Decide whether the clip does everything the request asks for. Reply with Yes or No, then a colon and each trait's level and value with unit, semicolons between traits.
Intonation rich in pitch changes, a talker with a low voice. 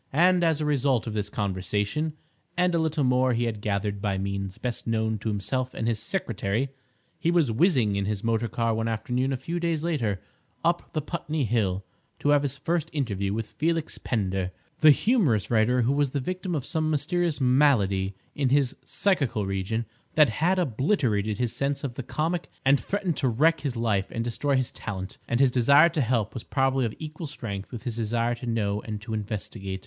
Yes: wide, 5.8 semitones; low, 125 Hz